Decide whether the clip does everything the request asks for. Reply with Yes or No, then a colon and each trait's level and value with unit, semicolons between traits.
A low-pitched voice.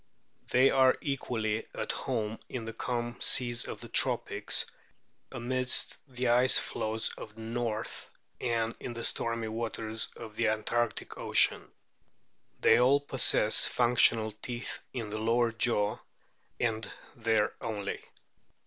Yes: low, 115 Hz